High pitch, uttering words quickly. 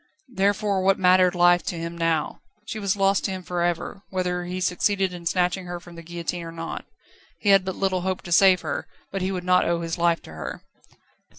No: medium, 180 Hz; fast, 220 wpm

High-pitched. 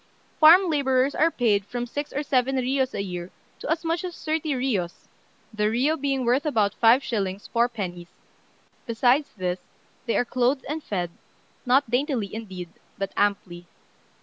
Yes: high, 245 Hz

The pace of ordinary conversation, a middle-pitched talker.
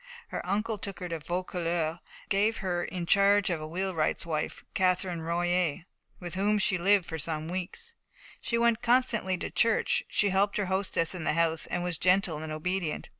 Yes: average, 185 wpm; medium, 180 Hz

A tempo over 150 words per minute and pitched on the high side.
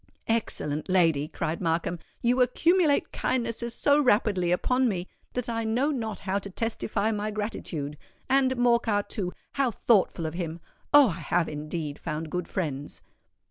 No: average, 145 wpm; high, 205 Hz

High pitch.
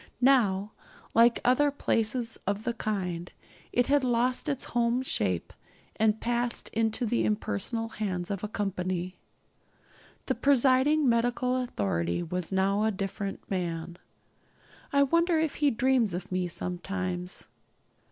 Yes: high, 215 Hz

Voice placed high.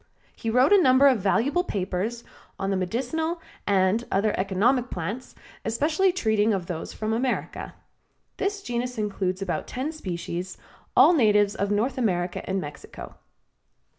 Yes: high, 220 Hz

